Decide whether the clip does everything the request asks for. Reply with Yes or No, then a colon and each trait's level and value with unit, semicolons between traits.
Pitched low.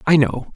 No: medium, 150 Hz